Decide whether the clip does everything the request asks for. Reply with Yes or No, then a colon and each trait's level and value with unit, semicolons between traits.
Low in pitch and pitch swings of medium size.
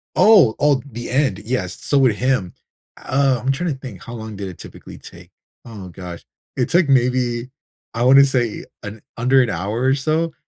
Yes: low, 125 Hz; average, 3.7 semitones